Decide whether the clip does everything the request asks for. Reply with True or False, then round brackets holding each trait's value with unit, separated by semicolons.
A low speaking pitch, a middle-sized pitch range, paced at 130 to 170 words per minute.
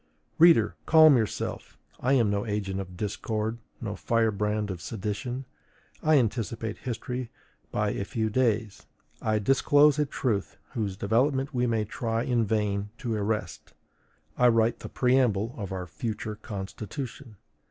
True (110 Hz; 3.2 semitones; 140 wpm)